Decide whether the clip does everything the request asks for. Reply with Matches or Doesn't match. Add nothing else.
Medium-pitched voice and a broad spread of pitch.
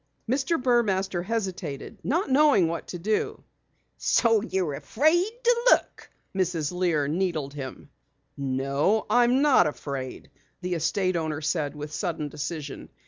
Matches